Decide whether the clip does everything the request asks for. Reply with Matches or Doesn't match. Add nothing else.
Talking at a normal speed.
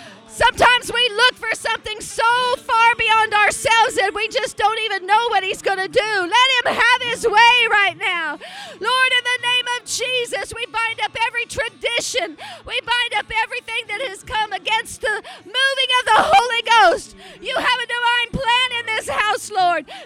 Matches